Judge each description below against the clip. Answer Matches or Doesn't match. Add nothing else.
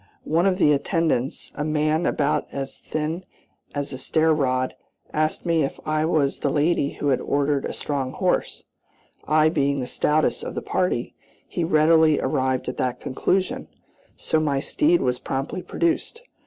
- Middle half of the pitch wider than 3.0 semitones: Doesn't match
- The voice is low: Doesn't match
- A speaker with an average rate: Matches